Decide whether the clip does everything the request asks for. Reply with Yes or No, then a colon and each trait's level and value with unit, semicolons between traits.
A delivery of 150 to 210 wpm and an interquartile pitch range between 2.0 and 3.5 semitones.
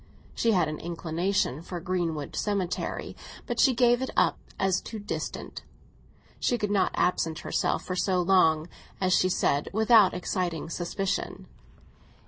No: average, 140 wpm; average, 3.2 semitones